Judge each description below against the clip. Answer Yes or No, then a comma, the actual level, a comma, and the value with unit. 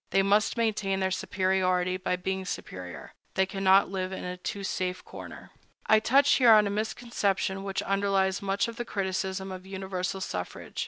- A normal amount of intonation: No, narrow, 1.3 semitones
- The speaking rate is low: No, average, 165 wpm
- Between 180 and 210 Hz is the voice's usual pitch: Yes, high, 190 Hz